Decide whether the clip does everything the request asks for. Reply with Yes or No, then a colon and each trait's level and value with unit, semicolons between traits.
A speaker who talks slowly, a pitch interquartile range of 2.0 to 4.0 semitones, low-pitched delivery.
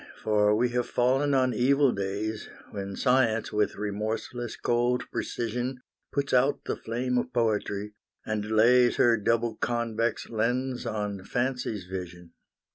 Yes: slow, 130 wpm; average, 2.8 semitones; low, 115 Hz